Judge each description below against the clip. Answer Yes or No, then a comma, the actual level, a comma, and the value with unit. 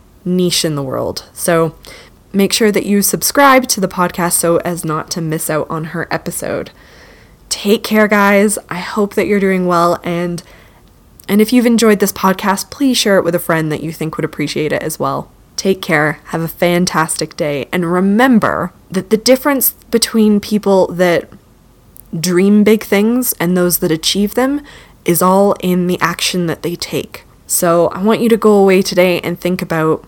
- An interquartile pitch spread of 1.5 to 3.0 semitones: No, average, 3.6 semitones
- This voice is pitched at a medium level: Yes, medium, 180 Hz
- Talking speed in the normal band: Yes, average, 185 wpm